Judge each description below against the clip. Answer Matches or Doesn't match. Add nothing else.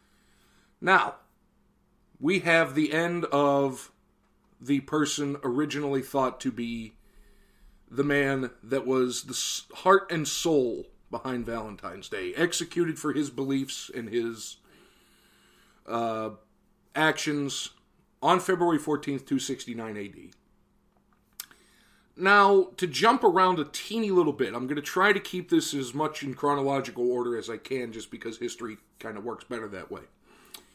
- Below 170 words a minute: Matches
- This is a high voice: Doesn't match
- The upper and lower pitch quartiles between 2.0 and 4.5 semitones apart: Doesn't match